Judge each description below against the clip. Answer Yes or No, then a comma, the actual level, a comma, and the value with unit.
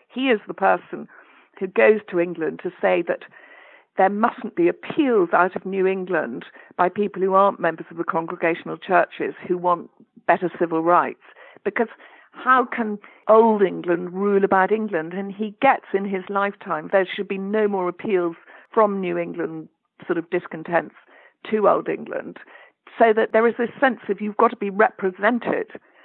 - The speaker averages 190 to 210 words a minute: No, average, 170 wpm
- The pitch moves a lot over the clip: No, average, 3.5 semitones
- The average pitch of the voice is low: No, high, 195 Hz